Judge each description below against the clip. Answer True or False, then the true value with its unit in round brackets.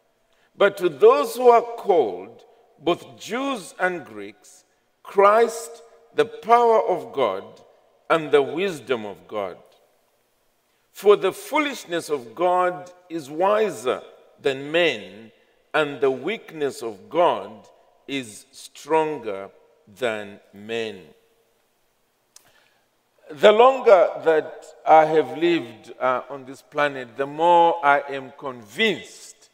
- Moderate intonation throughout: False (8.4 semitones)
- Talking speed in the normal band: False (110 wpm)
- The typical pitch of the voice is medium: True (170 Hz)